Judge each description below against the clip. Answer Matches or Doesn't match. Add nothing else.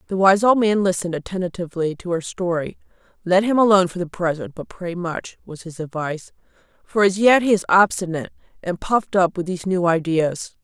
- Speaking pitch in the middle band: Matches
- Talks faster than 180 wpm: Matches